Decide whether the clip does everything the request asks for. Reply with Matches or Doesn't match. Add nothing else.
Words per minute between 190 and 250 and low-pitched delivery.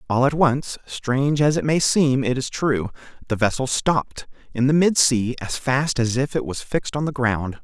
Matches